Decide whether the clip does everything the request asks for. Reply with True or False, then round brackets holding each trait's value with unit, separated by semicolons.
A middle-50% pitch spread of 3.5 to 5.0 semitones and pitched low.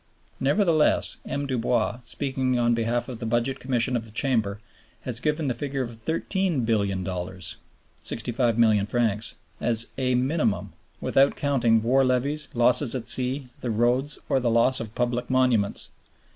False (2.8 semitones; 120 Hz)